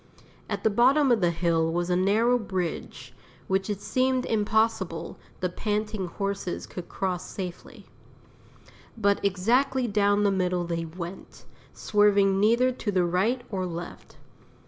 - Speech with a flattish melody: No, average, 3.5 semitones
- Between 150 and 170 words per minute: No, average, 140 wpm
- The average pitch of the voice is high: Yes, high, 200 Hz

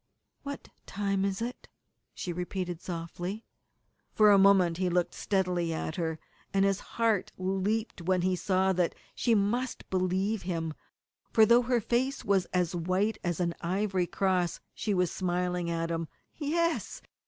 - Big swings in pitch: No, average, 2.8 semitones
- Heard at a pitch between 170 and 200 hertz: Yes, high, 190 Hz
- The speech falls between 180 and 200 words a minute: No, average, 155 wpm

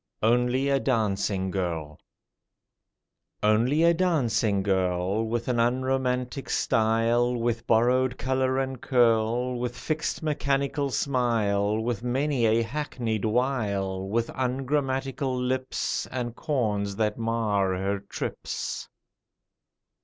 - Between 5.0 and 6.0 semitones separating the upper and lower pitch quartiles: No, average, 3.4 semitones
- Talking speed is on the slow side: Yes, slow, 105 wpm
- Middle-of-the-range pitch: No, low, 120 Hz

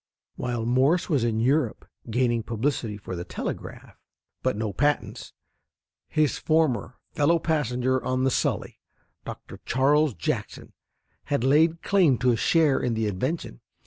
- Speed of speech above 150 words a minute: No, average, 140 wpm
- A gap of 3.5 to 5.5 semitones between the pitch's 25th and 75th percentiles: Yes, average, 4.4 semitones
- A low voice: Yes, low, 130 Hz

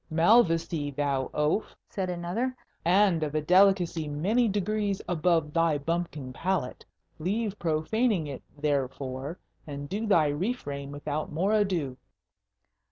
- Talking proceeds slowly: Yes, slow, 120 wpm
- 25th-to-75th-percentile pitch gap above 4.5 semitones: Yes, average, 5.1 semitones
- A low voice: No, medium, 165 Hz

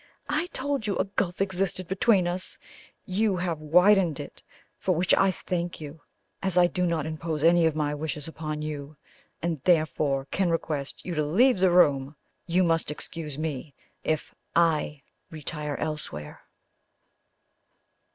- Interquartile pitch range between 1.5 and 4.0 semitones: Yes, average, 3.4 semitones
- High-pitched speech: No, medium, 165 Hz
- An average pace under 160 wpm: Yes, average, 150 wpm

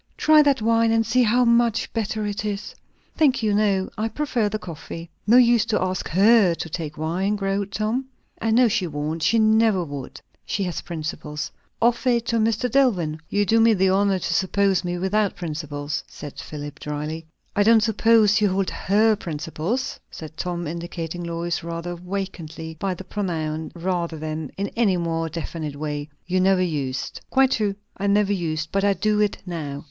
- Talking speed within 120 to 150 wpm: No, average, 185 wpm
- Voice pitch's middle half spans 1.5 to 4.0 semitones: No, average, 4.9 semitones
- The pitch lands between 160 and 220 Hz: Yes, high, 190 Hz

